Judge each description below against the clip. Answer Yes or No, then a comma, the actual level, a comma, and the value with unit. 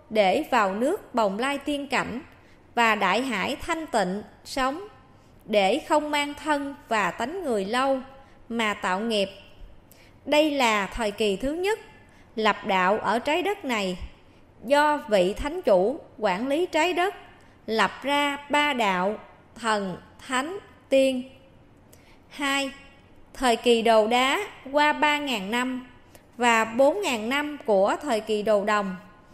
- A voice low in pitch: No, very high, 255 Hz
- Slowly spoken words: Yes, slow, 145 wpm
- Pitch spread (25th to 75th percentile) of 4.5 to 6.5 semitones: Yes, average, 5.3 semitones